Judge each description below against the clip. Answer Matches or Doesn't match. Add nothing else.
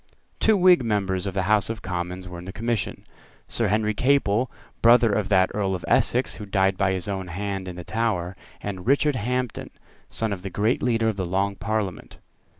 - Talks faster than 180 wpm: Matches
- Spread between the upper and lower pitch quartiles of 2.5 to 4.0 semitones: Matches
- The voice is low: Matches